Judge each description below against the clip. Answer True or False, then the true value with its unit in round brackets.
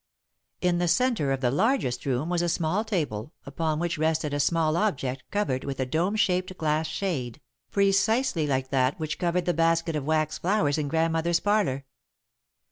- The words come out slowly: False (175 wpm)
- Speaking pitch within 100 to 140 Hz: False (160 Hz)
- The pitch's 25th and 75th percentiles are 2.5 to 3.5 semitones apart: False (4.0 semitones)